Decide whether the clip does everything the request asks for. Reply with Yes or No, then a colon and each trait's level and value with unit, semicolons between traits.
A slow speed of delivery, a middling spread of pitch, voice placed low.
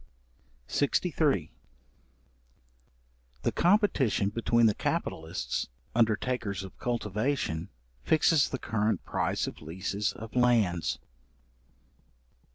Yes: slow, 80 wpm; average, 5.0 semitones; low, 110 Hz